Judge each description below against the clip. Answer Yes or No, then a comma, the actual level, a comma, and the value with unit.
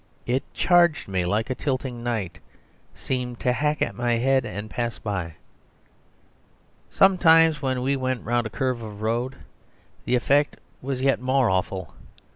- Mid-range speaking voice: No, low, 125 Hz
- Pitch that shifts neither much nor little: Yes, average, 3.4 semitones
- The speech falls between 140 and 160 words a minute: Yes, average, 150 wpm